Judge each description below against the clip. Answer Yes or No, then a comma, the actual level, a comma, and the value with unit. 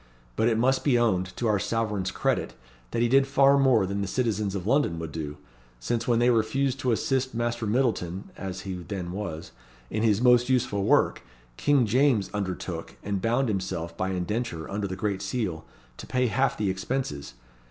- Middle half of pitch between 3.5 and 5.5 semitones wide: Yes, average, 4.8 semitones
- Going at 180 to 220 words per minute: Yes, average, 185 wpm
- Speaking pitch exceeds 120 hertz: No, low, 110 Hz